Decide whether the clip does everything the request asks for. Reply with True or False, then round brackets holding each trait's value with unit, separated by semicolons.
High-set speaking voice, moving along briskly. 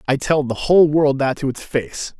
False (140 Hz; 245 wpm)